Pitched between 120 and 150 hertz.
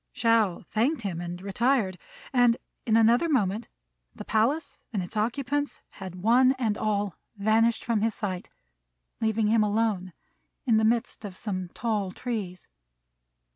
No: high, 220 Hz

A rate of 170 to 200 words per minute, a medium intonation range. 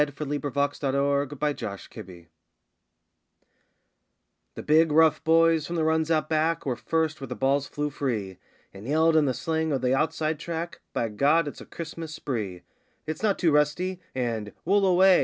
Yes: average, 175 wpm; average, 3.5 semitones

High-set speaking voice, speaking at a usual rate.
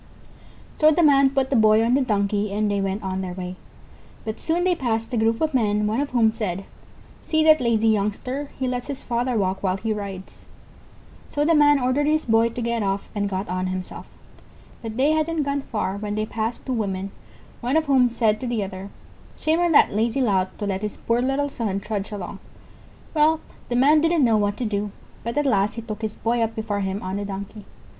No: high, 225 Hz; fast, 220 wpm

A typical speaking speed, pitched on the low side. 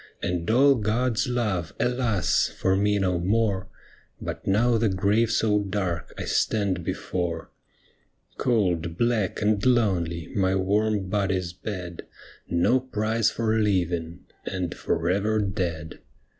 No: slow, 130 wpm; low, 100 Hz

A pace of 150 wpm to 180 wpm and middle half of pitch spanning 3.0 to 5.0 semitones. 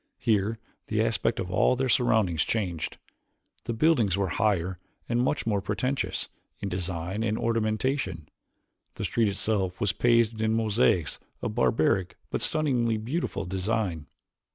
No: slow, 135 wpm; average, 3.8 semitones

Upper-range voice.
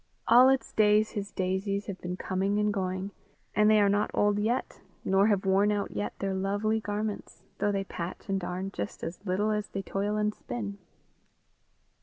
Yes: high, 200 Hz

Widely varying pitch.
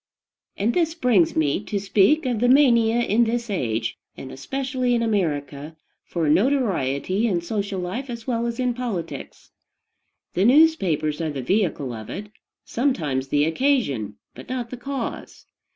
Yes: wide, 7.9 semitones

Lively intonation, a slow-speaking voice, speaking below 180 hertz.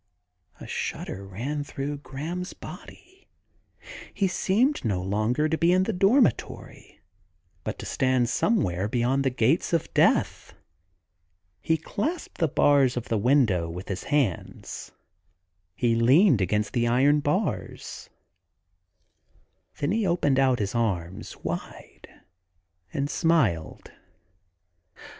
Yes: wide, 7.0 semitones; slow, 115 wpm; low, 135 Hz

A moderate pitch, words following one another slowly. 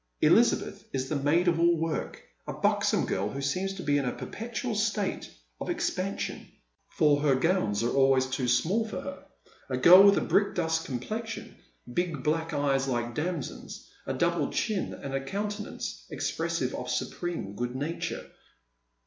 No: medium, 160 Hz; average, 160 wpm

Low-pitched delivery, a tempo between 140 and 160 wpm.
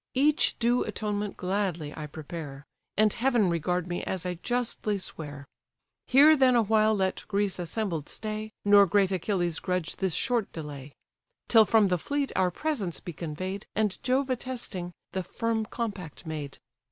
No: high, 195 Hz; average, 155 wpm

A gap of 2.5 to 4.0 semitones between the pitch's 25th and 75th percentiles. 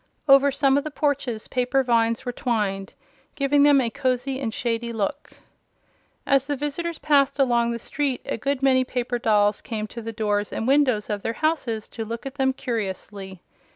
Yes: average, 3.6 semitones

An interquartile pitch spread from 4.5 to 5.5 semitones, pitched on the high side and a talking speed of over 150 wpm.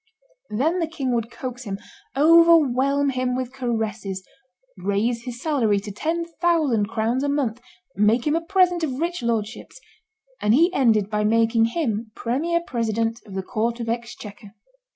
Yes: average, 5.0 semitones; high, 240 Hz; average, 160 wpm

